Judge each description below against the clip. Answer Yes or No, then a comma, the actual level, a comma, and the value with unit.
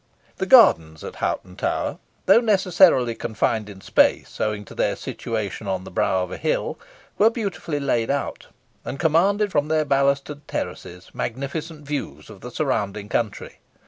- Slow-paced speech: No, average, 155 wpm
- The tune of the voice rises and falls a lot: Yes, wide, 7.2 semitones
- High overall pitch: No, medium, 140 Hz